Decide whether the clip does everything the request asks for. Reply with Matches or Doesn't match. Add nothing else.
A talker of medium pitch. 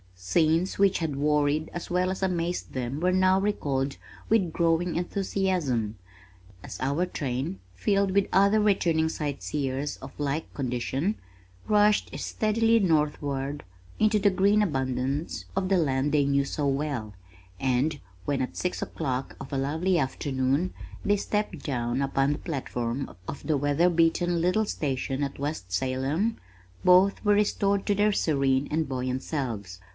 Matches